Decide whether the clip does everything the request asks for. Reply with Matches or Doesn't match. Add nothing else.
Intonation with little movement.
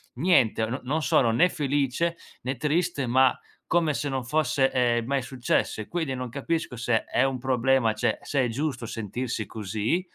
Doesn't match